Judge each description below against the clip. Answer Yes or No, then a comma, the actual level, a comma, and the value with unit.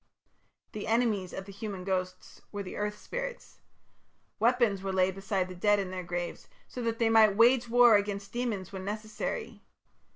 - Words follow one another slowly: No, average, 170 wpm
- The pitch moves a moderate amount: Yes, average, 3.2 semitones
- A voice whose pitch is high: Yes, high, 205 Hz